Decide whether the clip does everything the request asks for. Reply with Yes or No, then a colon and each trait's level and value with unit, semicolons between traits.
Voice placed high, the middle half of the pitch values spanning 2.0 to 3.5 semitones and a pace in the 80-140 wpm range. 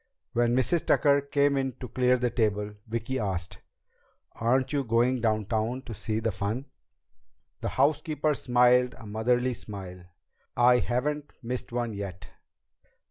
No: low, 120 Hz; average, 3.0 semitones; slow, 135 wpm